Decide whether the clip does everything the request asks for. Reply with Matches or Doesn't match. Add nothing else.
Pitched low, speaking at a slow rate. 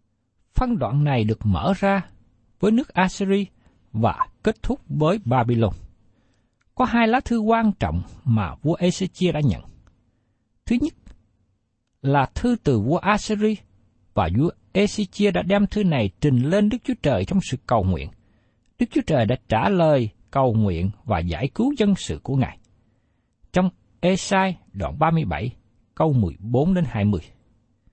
Matches